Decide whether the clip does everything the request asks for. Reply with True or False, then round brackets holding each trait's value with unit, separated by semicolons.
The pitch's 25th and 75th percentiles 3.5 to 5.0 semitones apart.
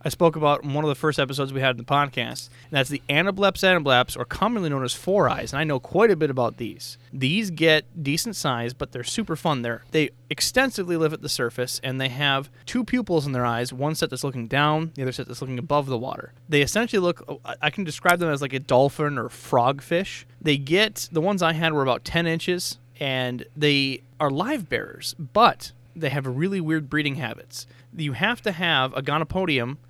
True (4.2 semitones)